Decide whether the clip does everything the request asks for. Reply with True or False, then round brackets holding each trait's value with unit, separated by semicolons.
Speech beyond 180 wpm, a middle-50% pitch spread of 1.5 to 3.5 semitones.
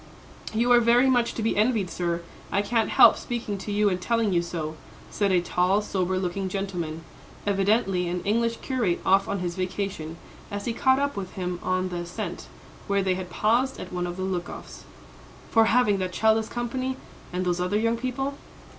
False (200 wpm; 4.1 semitones)